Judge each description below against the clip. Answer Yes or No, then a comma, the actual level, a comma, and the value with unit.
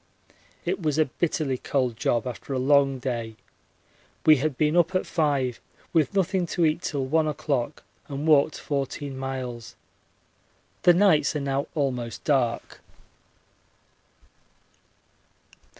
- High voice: No, medium, 140 Hz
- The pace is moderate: No, slow, 125 wpm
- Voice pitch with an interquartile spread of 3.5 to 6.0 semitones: No, average, 3.1 semitones